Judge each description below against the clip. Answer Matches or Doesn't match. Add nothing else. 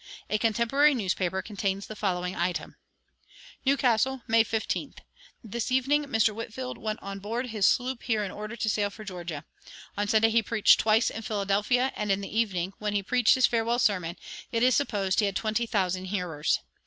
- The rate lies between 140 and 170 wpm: Doesn't match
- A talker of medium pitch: Doesn't match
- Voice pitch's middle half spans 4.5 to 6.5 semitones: Doesn't match